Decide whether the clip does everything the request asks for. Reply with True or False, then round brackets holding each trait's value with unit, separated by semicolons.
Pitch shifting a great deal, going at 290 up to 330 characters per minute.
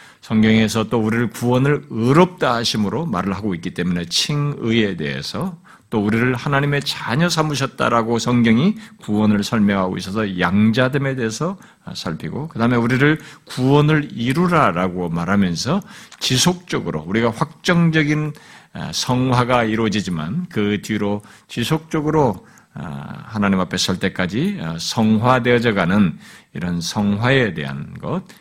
True (6.5 semitones; 305 characters per minute)